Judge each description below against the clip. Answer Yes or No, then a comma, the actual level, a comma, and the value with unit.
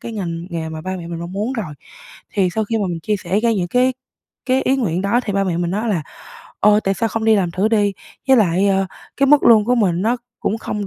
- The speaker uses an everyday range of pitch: Yes, average, 4.1 semitones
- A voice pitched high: Yes, high, 200 Hz